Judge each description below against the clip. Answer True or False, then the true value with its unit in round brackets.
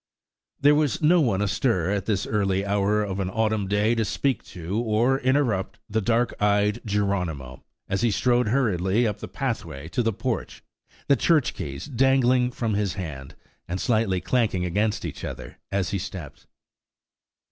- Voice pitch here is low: True (105 Hz)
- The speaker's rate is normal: True (165 wpm)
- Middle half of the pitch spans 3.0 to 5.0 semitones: True (4.0 semitones)